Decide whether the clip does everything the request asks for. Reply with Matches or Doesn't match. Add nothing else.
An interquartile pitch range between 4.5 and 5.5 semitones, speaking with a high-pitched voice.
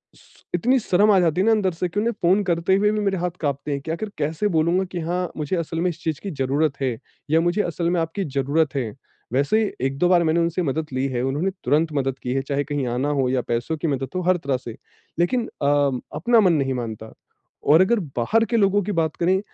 Doesn't match